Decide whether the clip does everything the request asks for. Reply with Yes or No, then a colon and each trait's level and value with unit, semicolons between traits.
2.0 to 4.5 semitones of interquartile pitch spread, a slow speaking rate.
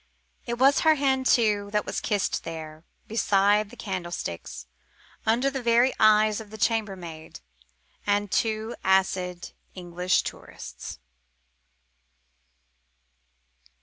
Yes: average, 4.1 semitones; slow, 105 wpm